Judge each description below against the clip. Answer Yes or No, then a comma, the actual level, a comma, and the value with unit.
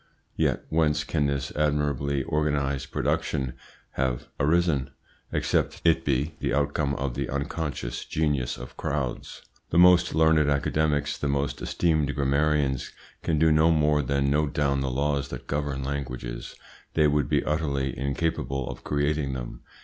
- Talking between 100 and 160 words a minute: Yes, average, 145 wpm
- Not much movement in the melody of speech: Yes, narrow, 1.9 semitones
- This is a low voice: Yes, very low, 70 Hz